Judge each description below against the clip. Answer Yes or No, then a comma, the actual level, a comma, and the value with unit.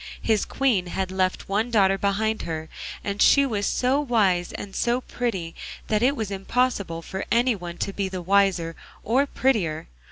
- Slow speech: No, average, 165 wpm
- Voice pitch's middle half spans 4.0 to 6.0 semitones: Yes, average, 4.3 semitones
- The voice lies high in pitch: Yes, high, 200 Hz